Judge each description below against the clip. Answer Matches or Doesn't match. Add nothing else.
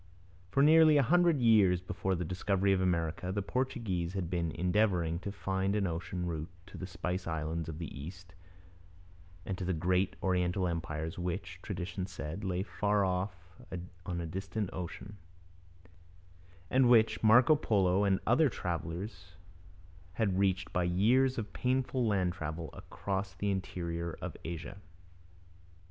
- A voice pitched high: Doesn't match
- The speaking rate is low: Doesn't match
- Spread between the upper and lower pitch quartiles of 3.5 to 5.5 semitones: Doesn't match